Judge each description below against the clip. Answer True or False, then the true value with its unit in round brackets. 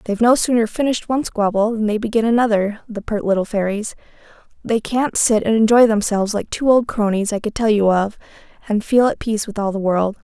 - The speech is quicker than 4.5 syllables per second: True (6.0 syllables/s)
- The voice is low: False (220 Hz)